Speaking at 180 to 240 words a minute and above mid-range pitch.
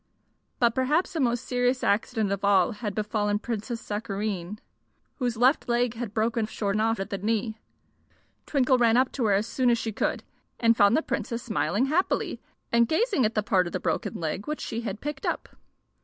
Yes: average, 195 wpm; high, 225 Hz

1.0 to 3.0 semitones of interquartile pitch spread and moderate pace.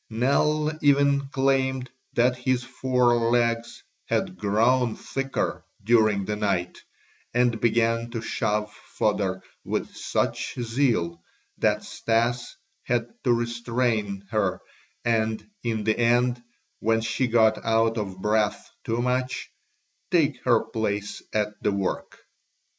No: narrow, 2.6 semitones; slow, 120 wpm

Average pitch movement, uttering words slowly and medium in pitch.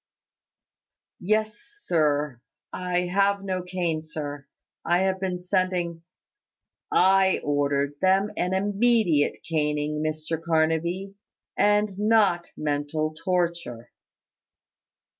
Yes: average, 3.7 semitones; slow, 95 wpm; medium, 175 Hz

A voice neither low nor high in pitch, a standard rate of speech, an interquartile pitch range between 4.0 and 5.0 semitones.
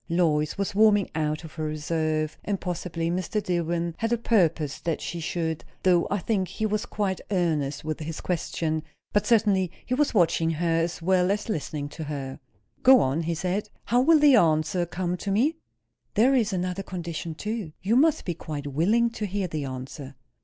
Yes: medium, 175 Hz; average, 190 wpm; average, 4.6 semitones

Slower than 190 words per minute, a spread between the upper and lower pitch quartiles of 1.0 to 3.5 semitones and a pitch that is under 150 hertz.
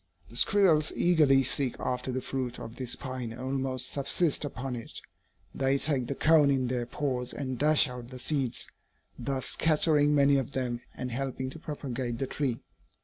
Yes: average, 175 wpm; narrow, 2.5 semitones; low, 135 Hz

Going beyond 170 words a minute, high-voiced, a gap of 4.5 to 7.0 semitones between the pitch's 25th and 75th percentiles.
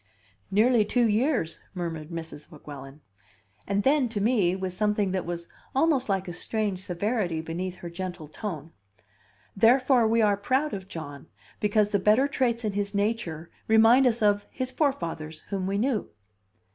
No: average, 160 wpm; high, 200 Hz; average, 4.9 semitones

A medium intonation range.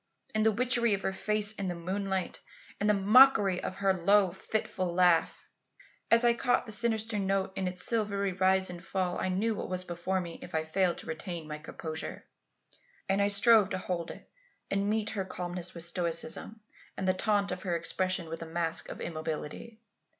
Yes: average, 3.1 semitones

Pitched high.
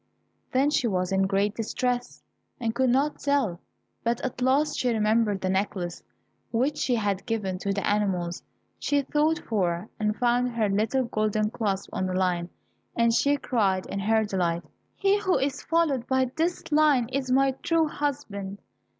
Yes: high, 230 Hz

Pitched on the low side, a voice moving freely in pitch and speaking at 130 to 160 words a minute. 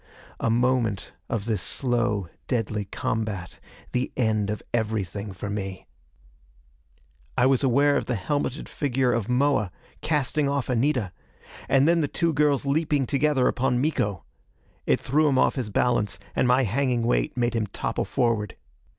No: low, 125 Hz; average, 4.5 semitones; average, 150 wpm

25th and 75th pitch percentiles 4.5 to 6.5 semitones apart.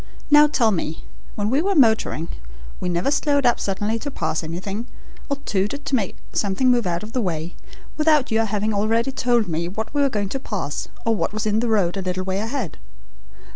Yes: average, 5.2 semitones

